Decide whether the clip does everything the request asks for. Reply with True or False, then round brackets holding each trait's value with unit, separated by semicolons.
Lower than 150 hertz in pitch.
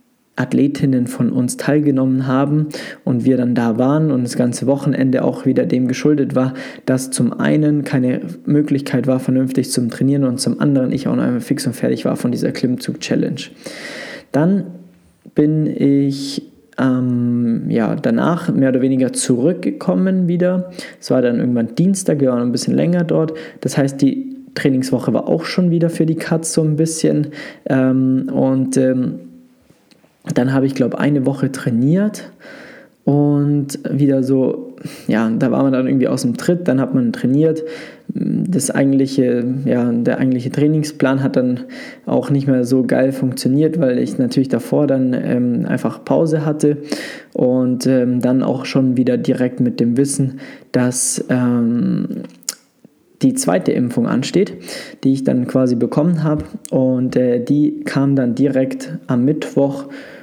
True (135 Hz)